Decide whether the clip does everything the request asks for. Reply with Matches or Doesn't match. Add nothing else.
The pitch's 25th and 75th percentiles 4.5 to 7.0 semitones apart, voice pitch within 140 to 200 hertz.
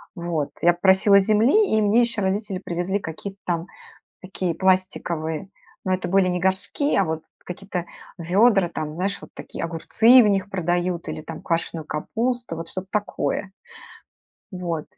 Doesn't match